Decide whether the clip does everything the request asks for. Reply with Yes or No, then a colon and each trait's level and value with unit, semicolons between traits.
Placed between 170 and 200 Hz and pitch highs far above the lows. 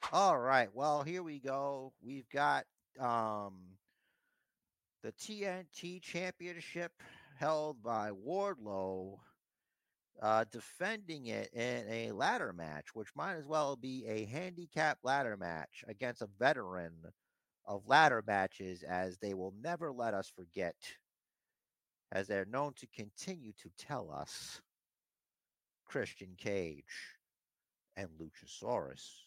No: low, 125 Hz; wide, 7.9 semitones